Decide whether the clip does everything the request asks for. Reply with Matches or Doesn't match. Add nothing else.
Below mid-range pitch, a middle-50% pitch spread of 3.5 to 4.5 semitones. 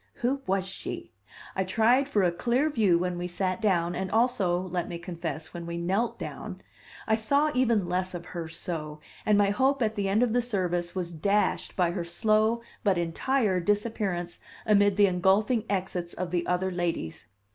Doesn't match